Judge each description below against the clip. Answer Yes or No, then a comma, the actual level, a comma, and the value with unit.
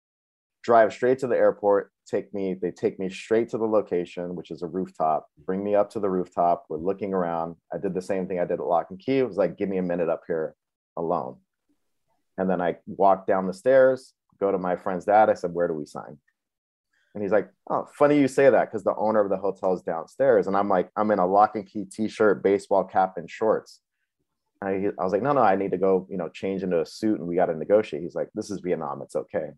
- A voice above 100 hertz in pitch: No, very low, 95 Hz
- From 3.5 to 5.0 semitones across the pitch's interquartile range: No, average, 2.8 semitones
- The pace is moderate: No, fast, 255 wpm